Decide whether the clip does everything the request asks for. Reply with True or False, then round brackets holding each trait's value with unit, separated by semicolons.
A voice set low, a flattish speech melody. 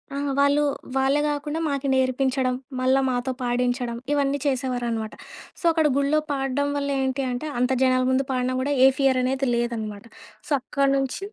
False (265 Hz; 2.0 semitones)